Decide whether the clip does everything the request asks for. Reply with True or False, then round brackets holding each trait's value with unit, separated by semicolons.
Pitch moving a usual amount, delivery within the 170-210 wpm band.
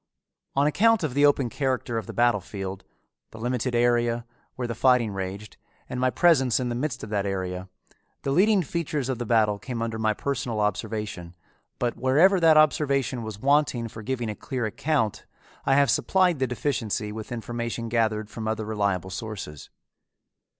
True (4.1 semitones; 175 wpm)